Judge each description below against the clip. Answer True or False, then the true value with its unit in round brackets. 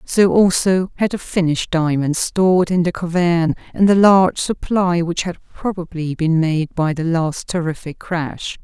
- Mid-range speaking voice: True (175 Hz)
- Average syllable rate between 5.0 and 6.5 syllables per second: False (4.5 syllables/s)